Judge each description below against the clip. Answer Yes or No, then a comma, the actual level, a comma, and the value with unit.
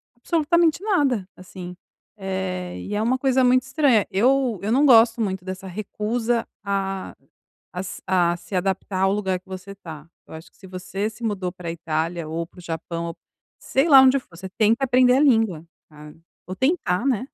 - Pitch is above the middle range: Yes, high, 195 Hz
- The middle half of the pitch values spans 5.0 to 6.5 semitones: Yes, wide, 5.5 semitones